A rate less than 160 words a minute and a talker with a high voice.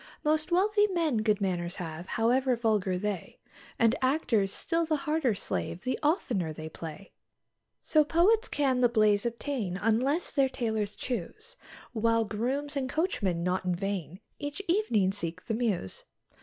Yes: average, 150 wpm; high, 230 Hz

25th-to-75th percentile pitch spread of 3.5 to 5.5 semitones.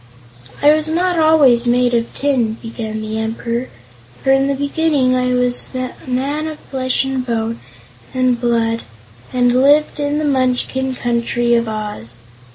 No: average, 3.0 semitones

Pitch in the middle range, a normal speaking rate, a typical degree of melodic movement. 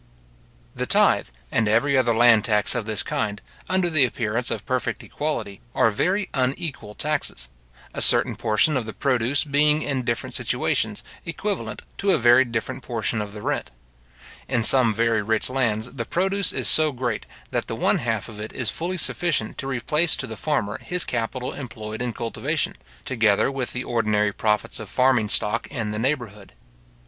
No: low, 120 Hz; average, 175 wpm; average, 4.6 semitones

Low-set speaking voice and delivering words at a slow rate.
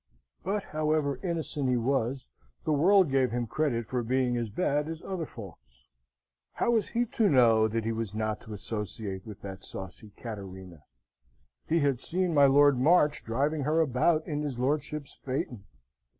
No: low, 130 Hz; average, 165 wpm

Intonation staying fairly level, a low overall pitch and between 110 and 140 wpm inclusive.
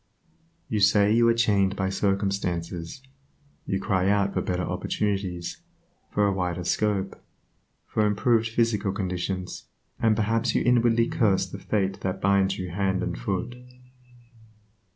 Yes: narrow, 2.3 semitones; low, 100 Hz; slow, 135 wpm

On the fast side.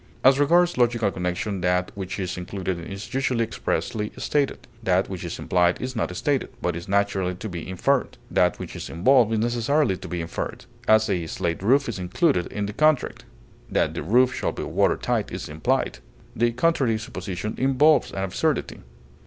No: average, 180 wpm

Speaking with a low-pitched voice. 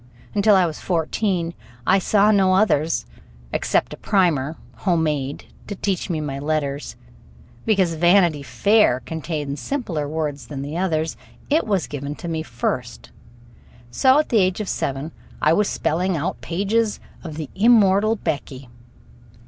No: medium, 170 Hz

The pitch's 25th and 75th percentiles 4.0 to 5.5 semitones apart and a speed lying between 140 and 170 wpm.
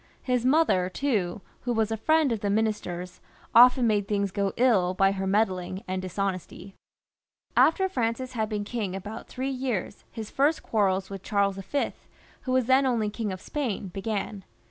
Yes: average, 4.4 semitones; average, 145 wpm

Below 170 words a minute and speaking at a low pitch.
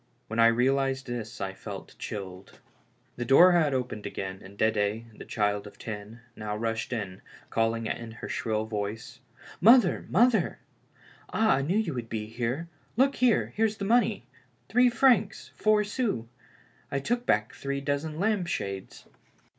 Yes: average, 160 wpm; low, 120 Hz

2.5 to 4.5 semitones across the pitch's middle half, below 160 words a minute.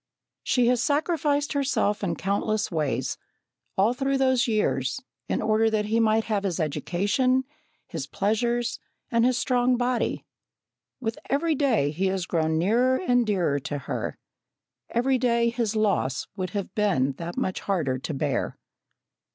No: average, 5.3 semitones; average, 150 wpm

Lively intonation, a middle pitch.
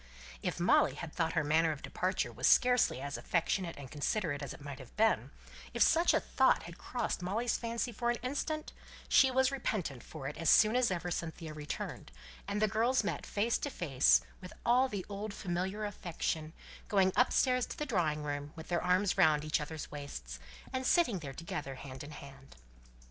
Yes: wide, 7.3 semitones; medium, 180 Hz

